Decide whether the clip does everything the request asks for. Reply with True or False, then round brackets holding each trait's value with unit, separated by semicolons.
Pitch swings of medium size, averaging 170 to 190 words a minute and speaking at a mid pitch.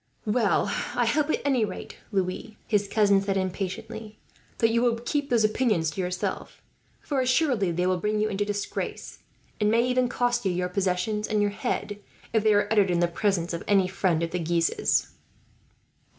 False (3.8 semitones; 185 wpm; 205 Hz)